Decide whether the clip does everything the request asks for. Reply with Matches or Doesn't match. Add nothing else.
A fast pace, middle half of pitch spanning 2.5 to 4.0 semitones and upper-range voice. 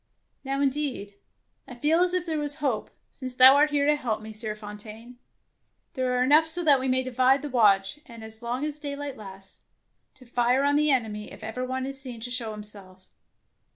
Doesn't match